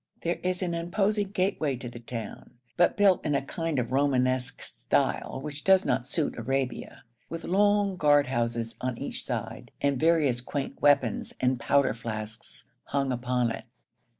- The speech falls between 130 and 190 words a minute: Yes, average, 160 wpm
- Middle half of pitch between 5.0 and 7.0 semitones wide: Yes, wide, 5.4 semitones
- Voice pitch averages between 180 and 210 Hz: No, medium, 140 Hz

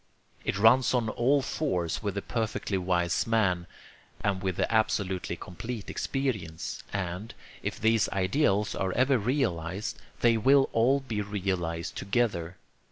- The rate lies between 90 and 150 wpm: Yes, slow, 135 wpm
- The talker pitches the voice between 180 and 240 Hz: No, low, 105 Hz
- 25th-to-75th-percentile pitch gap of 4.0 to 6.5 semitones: Yes, average, 4.6 semitones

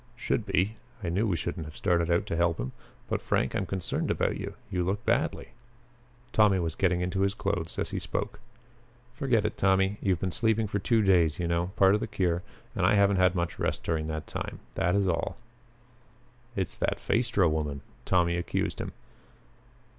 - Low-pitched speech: Yes, very low, 95 Hz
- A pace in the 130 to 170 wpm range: No, average, 190 wpm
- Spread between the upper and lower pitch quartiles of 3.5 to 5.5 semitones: No, average, 3.1 semitones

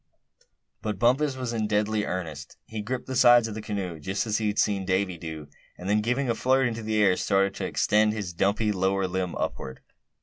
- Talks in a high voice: No, low, 105 Hz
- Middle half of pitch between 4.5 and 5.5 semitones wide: No, average, 3.2 semitones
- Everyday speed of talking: No, fast, 210 wpm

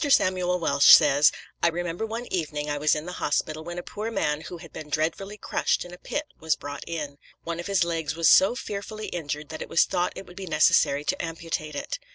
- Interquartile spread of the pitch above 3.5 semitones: No, average, 3.2 semitones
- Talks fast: Yes, fast, 225 wpm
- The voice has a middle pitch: Yes, medium, 165 Hz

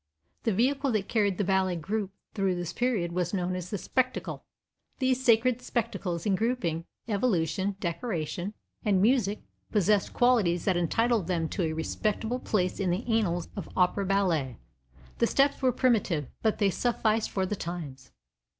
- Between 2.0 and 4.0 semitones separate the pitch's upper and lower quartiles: No, average, 4.5 semitones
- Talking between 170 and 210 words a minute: No, average, 155 wpm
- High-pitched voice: Yes, high, 195 Hz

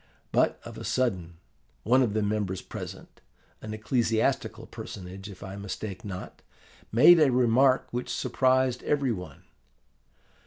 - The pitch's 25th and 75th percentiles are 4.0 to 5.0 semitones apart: Yes, average, 4.7 semitones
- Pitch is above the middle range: No, low, 110 Hz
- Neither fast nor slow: No, slow, 130 wpm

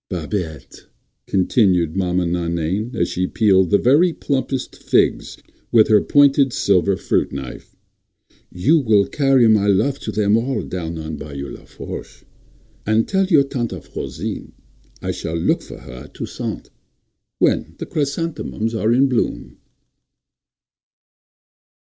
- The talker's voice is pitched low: Yes, low, 105 Hz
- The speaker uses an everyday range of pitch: No, wide, 6.9 semitones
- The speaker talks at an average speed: No, slow, 125 wpm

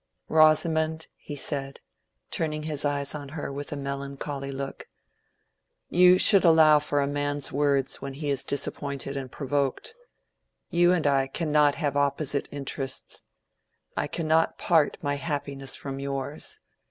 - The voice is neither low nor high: Yes, medium, 145 Hz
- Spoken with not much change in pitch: Yes, narrow, 1.9 semitones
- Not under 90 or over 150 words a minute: Yes, average, 140 wpm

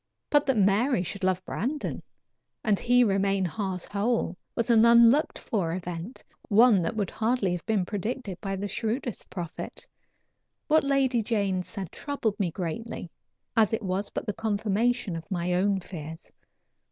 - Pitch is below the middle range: No, high, 205 Hz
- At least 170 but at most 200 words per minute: No, average, 155 wpm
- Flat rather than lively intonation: No, average, 4.1 semitones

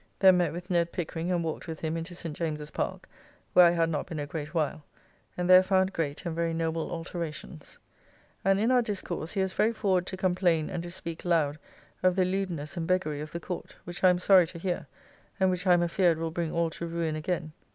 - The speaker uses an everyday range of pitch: No, narrow, 2.1 semitones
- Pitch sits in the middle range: Yes, medium, 170 Hz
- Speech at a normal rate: No, fast, 230 wpm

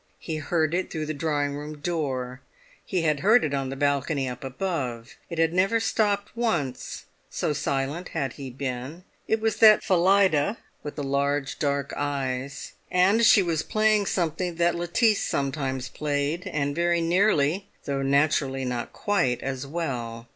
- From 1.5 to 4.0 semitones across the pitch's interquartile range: No, average, 4.6 semitones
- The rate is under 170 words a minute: Yes, average, 160 wpm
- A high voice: No, medium, 150 Hz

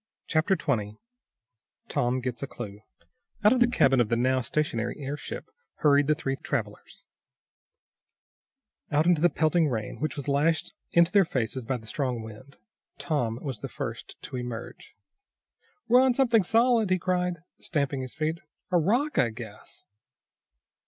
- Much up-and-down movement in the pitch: Yes, wide, 6.2 semitones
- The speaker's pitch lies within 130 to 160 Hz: Yes, medium, 140 Hz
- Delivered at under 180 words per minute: Yes, average, 150 wpm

